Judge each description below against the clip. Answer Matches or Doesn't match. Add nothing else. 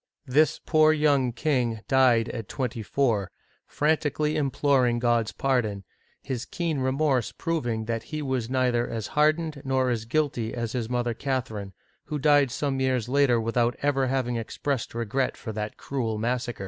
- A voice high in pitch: Doesn't match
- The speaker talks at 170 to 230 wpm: Doesn't match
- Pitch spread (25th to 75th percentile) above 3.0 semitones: Matches